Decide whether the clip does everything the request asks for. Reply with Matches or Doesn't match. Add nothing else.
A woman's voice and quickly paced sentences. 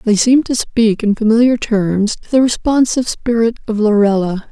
Doesn't match